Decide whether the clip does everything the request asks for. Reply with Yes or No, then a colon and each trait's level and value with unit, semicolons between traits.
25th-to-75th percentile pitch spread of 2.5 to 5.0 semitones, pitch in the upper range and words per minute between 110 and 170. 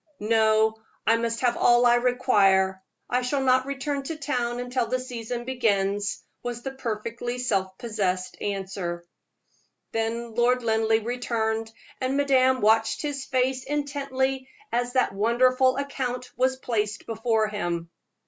Yes: average, 2.8 semitones; high, 240 Hz; slow, 135 wpm